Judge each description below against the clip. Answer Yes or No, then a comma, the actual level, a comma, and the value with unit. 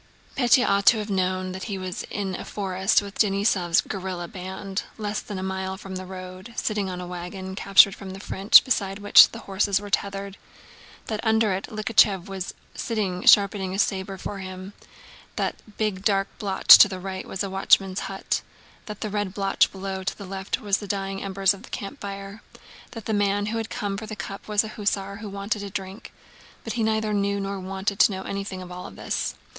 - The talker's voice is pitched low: No, high, 195 Hz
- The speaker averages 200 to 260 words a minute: Yes, fast, 205 wpm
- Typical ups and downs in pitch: No, narrow, 1.5 semitones